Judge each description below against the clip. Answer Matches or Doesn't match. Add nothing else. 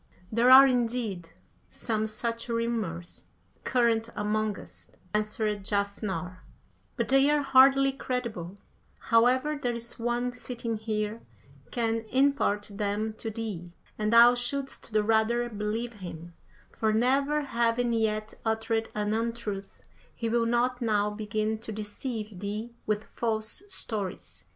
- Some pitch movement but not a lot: Doesn't match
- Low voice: Doesn't match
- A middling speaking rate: Doesn't match